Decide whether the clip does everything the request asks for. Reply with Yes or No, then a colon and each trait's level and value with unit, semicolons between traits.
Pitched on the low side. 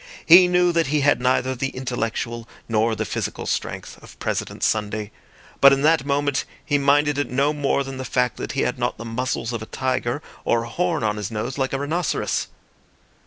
Yes: low, 130 Hz